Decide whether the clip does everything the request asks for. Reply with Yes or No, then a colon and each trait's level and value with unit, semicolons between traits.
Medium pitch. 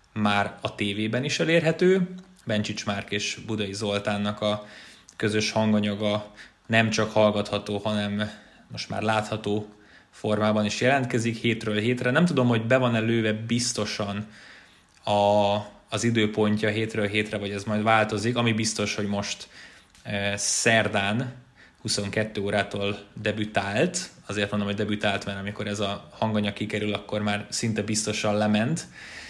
No: low, 105 Hz